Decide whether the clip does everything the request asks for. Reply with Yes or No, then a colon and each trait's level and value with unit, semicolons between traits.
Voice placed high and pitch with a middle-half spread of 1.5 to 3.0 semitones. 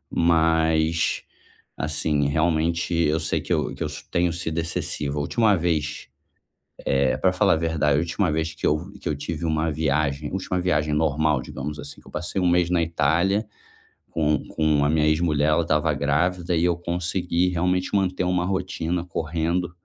No: very low, 80 Hz; narrow, 2.4 semitones